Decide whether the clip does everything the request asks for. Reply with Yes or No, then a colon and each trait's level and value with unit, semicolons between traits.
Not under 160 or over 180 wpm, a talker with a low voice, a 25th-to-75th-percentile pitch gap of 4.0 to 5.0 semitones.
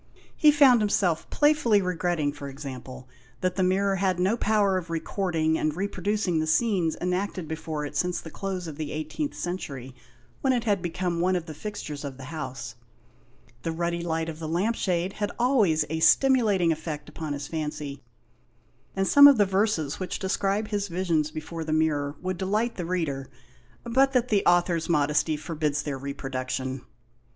No: average, 175 wpm; medium, 170 Hz; average, 4.4 semitones